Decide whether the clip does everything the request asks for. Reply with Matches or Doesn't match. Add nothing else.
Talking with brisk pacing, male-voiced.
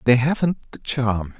Doesn't match